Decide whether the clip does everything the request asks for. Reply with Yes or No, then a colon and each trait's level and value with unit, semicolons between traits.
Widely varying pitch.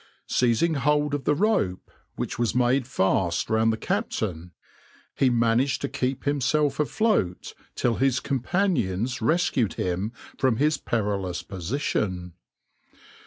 Yes: wide, 6.0 semitones